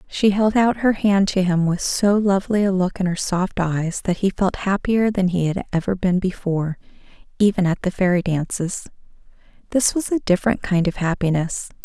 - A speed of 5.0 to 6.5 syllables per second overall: Yes, 5.1 syllables/s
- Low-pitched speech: No, high, 190 Hz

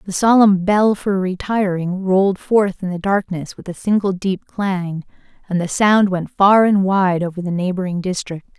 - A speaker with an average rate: Yes, average, 180 wpm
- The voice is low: No, high, 190 Hz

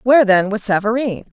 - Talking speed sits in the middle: Yes, average, 175 wpm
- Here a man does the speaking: No, female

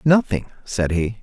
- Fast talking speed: No, average, 145 wpm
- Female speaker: No, male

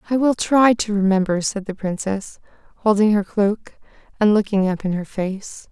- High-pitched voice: Yes, high, 205 Hz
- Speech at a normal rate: Yes, average, 180 wpm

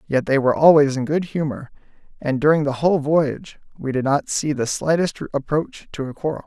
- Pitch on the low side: No, medium, 145 Hz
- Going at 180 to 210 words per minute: Yes, fast, 205 wpm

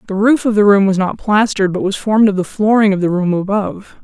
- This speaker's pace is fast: Yes, fast, 270 wpm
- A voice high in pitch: Yes, high, 200 Hz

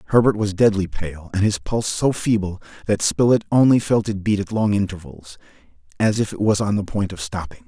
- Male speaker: Yes, male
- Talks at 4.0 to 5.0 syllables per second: No, 5.6 syllables/s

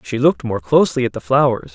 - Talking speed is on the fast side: Yes, fast, 240 wpm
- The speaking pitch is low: Yes, low, 120 Hz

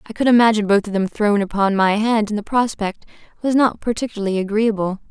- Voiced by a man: No, female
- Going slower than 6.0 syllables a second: No, 6.1 syllables/s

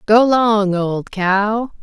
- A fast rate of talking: No, slow, 130 wpm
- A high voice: Yes, high, 210 Hz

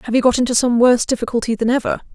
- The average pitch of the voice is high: Yes, high, 240 Hz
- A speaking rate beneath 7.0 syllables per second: No, 8.0 syllables/s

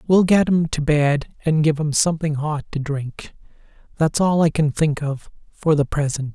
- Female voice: No, male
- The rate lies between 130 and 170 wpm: No, average, 190 wpm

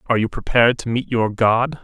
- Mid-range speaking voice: No, low, 115 Hz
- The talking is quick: Yes, fast, 230 wpm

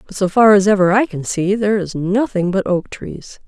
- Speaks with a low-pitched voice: No, high, 195 Hz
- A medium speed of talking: No, fast, 240 wpm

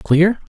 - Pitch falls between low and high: Yes, medium, 180 Hz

